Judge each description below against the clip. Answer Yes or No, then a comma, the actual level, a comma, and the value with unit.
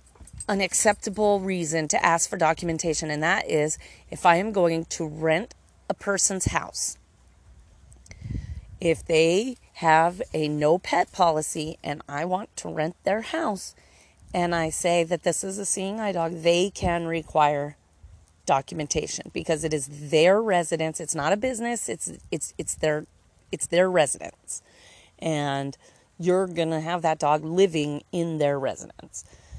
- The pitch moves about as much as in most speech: Yes, average, 3.5 semitones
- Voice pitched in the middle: Yes, medium, 165 Hz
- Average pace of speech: Yes, average, 150 wpm